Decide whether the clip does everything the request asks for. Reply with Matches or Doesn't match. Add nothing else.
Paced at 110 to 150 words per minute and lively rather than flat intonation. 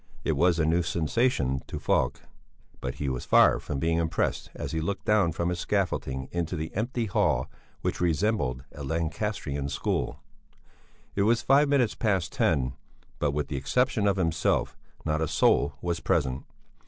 Doesn't match